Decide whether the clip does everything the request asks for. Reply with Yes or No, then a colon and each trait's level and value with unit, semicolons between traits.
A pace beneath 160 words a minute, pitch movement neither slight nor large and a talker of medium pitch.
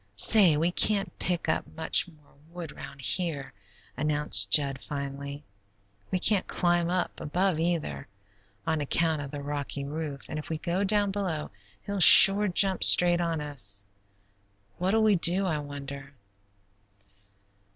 Yes: average, 140 wpm; average, 4.1 semitones; medium, 160 Hz